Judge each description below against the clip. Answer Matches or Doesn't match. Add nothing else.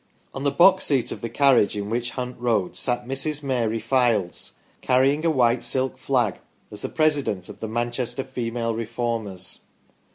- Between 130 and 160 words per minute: Doesn't match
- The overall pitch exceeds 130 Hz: Doesn't match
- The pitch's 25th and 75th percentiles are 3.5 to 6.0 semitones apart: Doesn't match